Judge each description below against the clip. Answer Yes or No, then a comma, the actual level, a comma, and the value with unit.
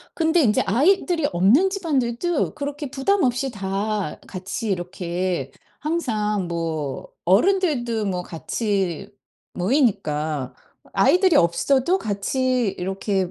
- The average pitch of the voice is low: No, high, 215 Hz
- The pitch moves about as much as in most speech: No, wide, 7.6 semitones